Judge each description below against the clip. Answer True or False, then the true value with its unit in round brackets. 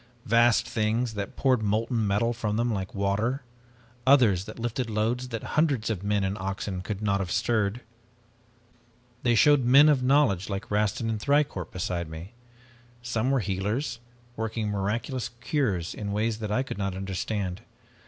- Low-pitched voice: True (110 Hz)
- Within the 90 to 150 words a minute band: False (165 wpm)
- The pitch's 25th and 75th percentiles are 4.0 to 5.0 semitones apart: False (3.6 semitones)